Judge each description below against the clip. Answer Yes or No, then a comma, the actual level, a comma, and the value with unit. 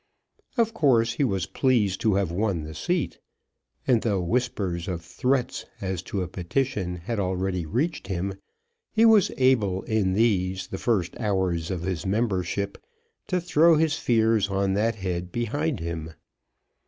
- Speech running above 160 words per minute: No, average, 155 wpm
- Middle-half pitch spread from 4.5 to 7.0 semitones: Yes, average, 5.1 semitones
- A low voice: Yes, low, 100 Hz